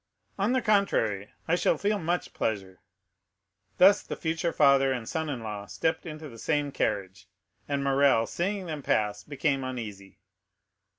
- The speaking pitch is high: No, medium, 140 Hz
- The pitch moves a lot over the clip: Yes, wide, 7.0 semitones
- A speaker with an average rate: Yes, average, 155 wpm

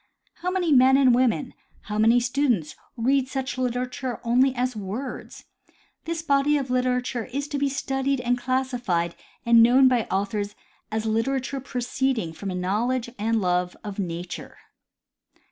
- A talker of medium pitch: No, very high, 250 Hz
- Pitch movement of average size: Yes, average, 3.6 semitones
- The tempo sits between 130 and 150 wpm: Yes, average, 145 wpm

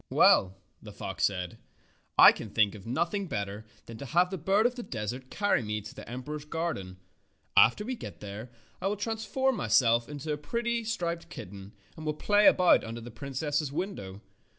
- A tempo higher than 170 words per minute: Yes, average, 195 wpm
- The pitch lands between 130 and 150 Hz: Yes, medium, 140 Hz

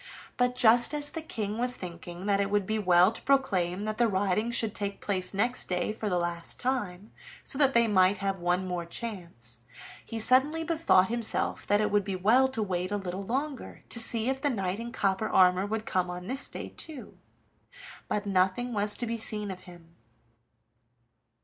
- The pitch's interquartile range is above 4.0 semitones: Yes, average, 4.4 semitones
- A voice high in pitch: Yes, high, 205 Hz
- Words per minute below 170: No, average, 195 wpm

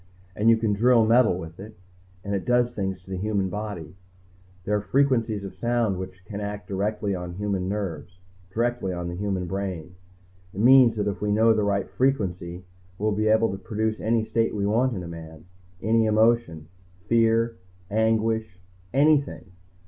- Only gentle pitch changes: No, average, 3.2 semitones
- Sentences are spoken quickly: No, average, 175 wpm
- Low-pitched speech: Yes, low, 105 Hz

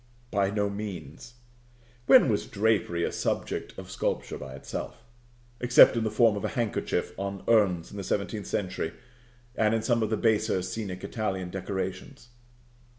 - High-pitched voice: No, low, 100 Hz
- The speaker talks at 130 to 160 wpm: Yes, average, 155 wpm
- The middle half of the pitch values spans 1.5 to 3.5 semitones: Yes, average, 3.1 semitones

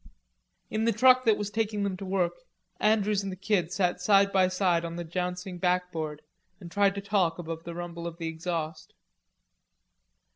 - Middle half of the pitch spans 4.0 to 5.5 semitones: No, average, 2.9 semitones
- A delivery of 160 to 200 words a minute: Yes, average, 180 wpm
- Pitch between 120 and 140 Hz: No, medium, 180 Hz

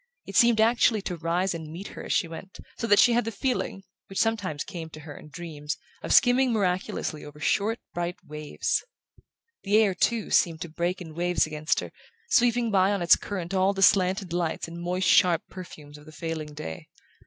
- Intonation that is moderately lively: Yes, average, 4.0 semitones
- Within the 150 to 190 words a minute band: No, average, 200 wpm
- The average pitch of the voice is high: No, medium, 180 Hz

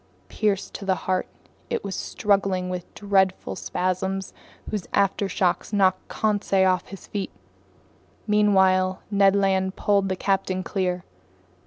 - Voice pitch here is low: No, high, 190 Hz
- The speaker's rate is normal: No, slow, 125 wpm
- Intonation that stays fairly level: Yes, narrow, 1.3 semitones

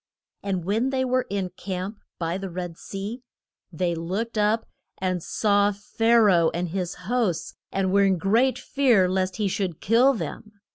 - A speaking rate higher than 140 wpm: Yes, average, 175 wpm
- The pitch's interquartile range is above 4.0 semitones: No, average, 3.6 semitones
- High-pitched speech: Yes, high, 195 Hz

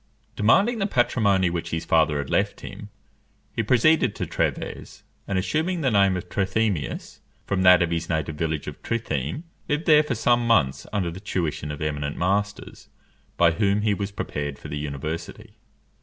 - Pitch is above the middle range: No, very low, 95 Hz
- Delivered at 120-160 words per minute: No, average, 170 wpm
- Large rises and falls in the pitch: Yes, wide, 6.0 semitones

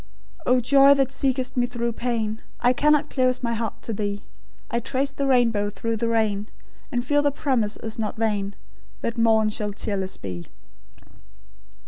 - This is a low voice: No, high, 235 Hz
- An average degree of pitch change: Yes, average, 3.3 semitones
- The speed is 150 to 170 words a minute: Yes, average, 165 wpm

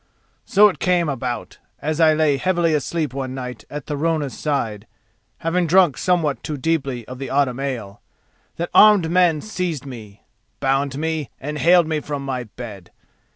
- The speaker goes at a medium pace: Yes, average, 160 wpm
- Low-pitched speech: No, medium, 145 Hz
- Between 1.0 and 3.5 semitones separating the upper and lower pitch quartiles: No, average, 4.1 semitones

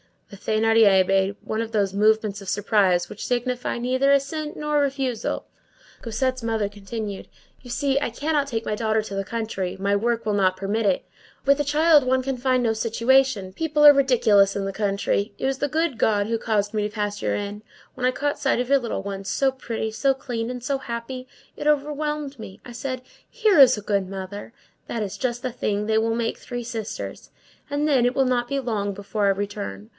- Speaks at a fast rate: Yes, fast, 210 wpm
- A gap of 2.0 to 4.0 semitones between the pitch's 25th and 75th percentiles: No, average, 4.6 semitones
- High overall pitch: Yes, high, 230 Hz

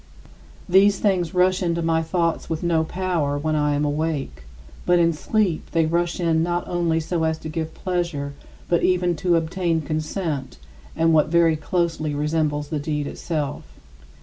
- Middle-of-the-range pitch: Yes, medium, 165 Hz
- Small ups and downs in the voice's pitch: Yes, narrow, 2.2 semitones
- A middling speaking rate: Yes, average, 165 wpm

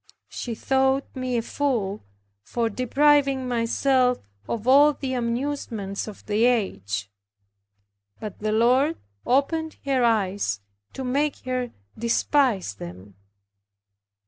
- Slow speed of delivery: Yes, slow, 110 wpm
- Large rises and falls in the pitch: No, average, 4.0 semitones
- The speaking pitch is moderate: No, high, 245 Hz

